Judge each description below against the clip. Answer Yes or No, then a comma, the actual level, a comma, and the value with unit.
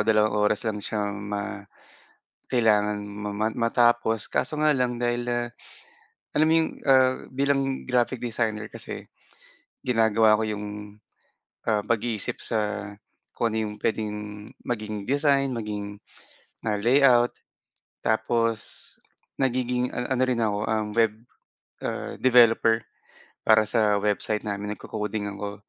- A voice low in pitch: Yes, low, 110 Hz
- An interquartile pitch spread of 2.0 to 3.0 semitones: Yes, narrow, 2.6 semitones